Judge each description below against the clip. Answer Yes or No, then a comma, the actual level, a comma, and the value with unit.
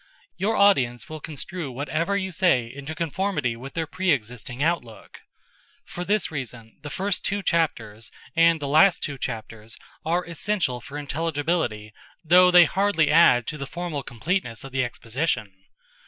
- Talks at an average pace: Yes, average, 155 wpm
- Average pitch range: No, wide, 6.1 semitones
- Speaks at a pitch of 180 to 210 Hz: No, medium, 150 Hz